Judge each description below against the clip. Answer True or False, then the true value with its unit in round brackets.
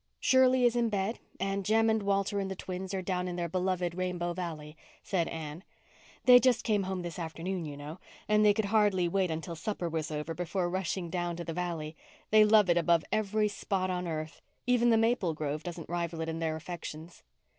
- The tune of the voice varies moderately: True (3.5 semitones)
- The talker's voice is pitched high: False (180 Hz)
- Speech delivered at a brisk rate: True (210 wpm)